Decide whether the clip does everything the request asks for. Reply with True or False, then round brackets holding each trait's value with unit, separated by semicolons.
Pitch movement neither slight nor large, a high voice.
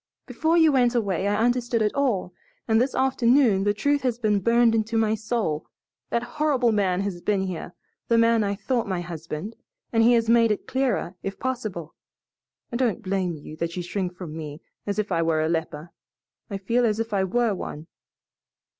True (4.7 semitones; 215 Hz)